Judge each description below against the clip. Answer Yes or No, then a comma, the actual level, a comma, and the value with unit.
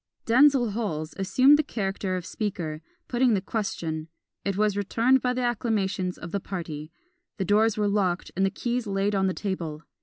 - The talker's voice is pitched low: No, high, 200 Hz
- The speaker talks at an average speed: Yes, average, 180 wpm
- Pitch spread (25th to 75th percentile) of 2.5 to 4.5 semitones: Yes, average, 3.8 semitones